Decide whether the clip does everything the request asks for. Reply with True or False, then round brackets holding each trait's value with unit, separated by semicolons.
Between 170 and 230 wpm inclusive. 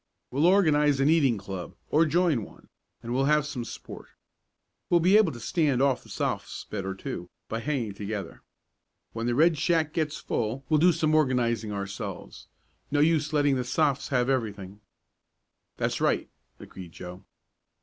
False (160 wpm)